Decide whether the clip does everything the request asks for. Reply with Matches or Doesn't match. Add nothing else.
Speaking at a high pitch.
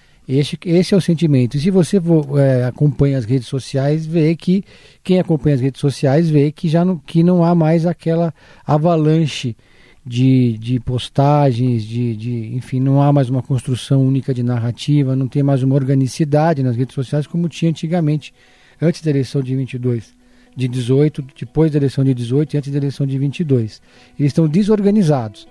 Doesn't match